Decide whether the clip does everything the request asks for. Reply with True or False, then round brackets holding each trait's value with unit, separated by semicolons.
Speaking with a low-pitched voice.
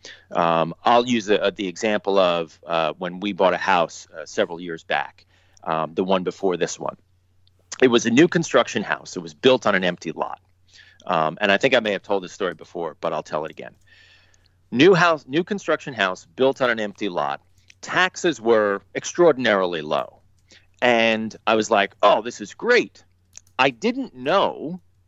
True (100 Hz)